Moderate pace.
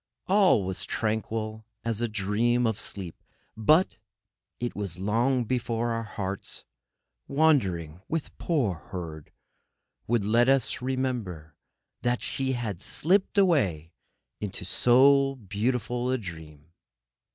No: slow, 115 wpm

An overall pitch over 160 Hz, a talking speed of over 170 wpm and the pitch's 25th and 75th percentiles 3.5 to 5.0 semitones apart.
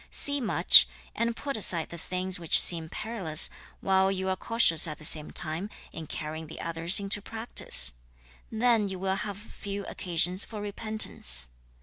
No: high, 190 Hz; average, 160 wpm; average, 4.6 semitones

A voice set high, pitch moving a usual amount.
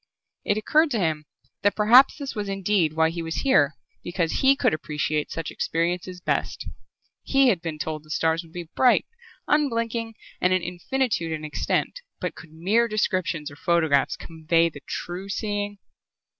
No: medium, 175 Hz; average, 5.0 semitones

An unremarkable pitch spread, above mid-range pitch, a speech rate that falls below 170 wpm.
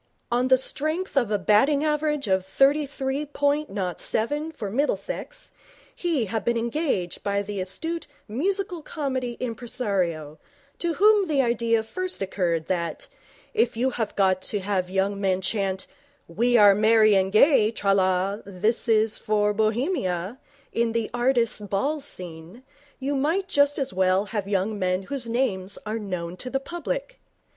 No: wide, 6.3 semitones; high, 225 Hz; average, 160 wpm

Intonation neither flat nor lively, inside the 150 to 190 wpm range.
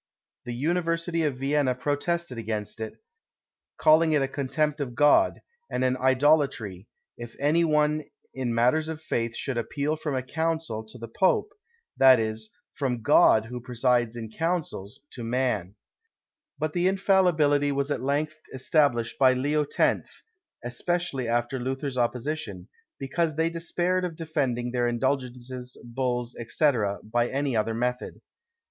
No: average, 4.4 semitones; average, 140 wpm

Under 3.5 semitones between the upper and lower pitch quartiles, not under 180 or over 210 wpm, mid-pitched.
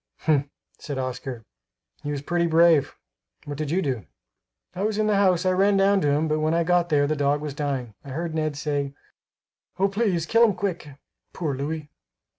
No: average, 4.1 semitones; average, 200 wpm; medium, 155 Hz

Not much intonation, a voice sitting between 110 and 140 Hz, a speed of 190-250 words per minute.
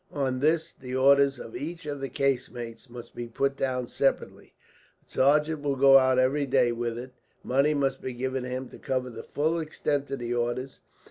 Yes: narrow, 2.0 semitones; low, 135 Hz; average, 200 wpm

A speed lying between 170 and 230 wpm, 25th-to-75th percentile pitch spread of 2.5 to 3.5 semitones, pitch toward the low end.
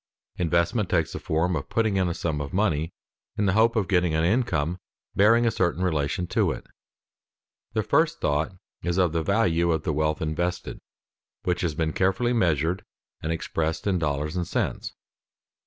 Yes: average, 175 wpm; average, 3.2 semitones; very low, 85 Hz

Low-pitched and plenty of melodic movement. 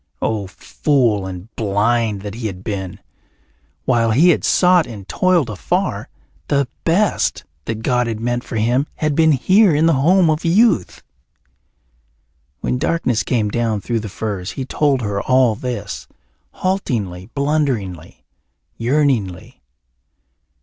Yes: low, 120 Hz; wide, 6.3 semitones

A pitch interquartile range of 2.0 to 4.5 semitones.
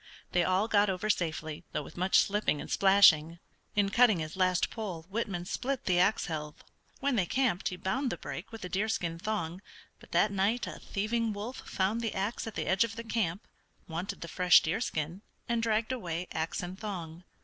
Yes: average, 4.2 semitones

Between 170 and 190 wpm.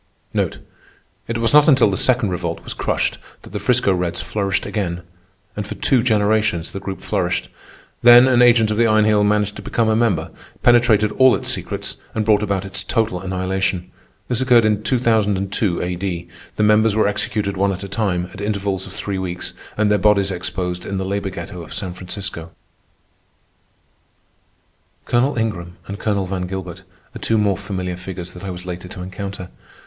Yes: average, 180 wpm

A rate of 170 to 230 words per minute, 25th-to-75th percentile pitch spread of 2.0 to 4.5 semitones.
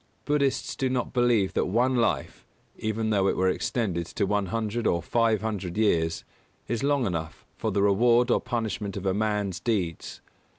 Yes: average, 175 wpm; average, 3.7 semitones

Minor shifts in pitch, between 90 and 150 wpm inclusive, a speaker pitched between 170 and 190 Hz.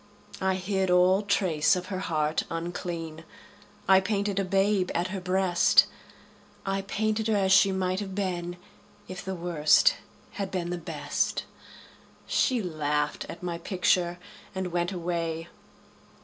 Yes: narrow, 2.1 semitones; average, 140 wpm; medium, 185 Hz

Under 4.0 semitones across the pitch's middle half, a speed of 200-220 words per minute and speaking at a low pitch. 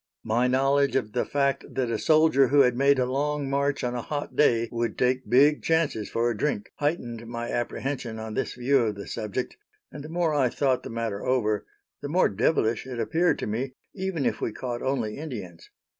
Yes: average, 3.5 semitones; fast, 205 wpm; low, 130 Hz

